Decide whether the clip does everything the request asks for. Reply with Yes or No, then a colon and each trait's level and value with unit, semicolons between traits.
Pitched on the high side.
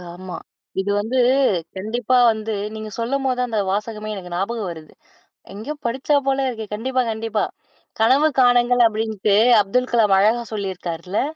Yes: high, 220 Hz